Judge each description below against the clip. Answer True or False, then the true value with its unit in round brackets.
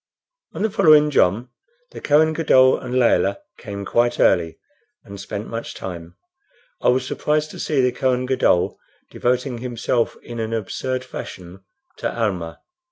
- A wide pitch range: False (4.6 semitones)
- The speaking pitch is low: True (120 Hz)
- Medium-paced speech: True (150 wpm)